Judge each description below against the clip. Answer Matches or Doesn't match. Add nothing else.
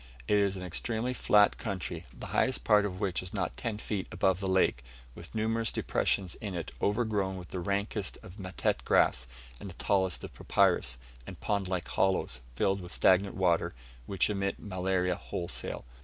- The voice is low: Matches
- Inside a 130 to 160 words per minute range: Doesn't match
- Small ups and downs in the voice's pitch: Matches